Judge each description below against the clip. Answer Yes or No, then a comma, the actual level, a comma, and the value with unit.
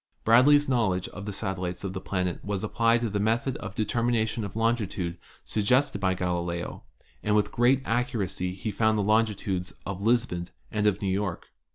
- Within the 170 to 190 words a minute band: Yes, average, 180 wpm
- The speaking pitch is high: No, low, 105 Hz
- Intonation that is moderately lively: Yes, average, 3.6 semitones